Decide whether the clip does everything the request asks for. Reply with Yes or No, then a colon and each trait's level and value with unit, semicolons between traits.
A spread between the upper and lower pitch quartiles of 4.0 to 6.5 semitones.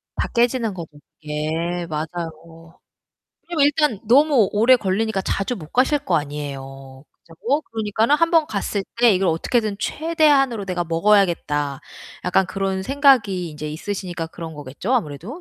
No: wide, 7.2 semitones